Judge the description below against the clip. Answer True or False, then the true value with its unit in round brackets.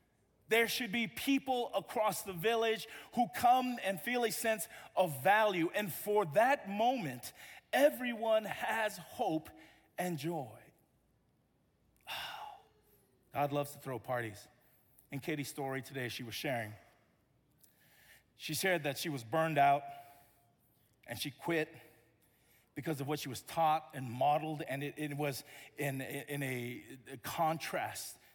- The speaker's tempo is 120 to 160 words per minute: True (135 wpm)